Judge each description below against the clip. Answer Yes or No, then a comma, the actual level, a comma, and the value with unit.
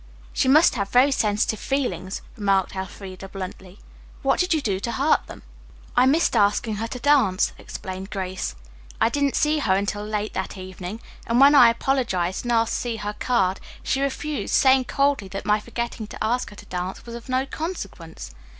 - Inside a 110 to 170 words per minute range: No, average, 185 wpm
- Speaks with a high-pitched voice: Yes, high, 220 Hz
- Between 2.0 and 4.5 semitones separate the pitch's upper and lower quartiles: No, wide, 5.4 semitones